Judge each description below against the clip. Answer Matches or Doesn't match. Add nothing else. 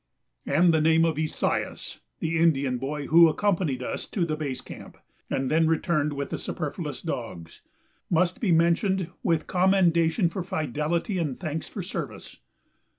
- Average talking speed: Matches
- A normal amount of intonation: Doesn't match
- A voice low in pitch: Doesn't match